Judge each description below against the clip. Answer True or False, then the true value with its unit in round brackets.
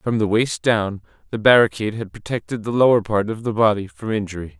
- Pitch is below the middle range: True (105 Hz)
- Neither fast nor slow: False (210 wpm)